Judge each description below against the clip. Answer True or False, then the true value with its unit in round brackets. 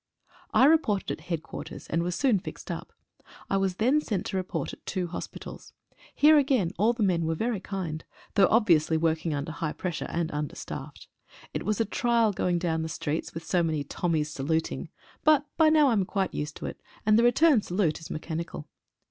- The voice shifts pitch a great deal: True (5.7 semitones)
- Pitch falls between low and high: True (180 Hz)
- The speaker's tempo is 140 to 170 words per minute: False (195 wpm)